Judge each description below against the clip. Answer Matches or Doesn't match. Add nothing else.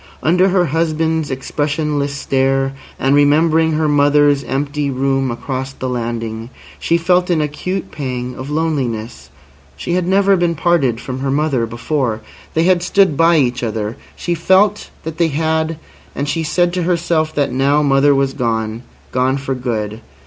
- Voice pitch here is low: Doesn't match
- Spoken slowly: Doesn't match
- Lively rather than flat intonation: Doesn't match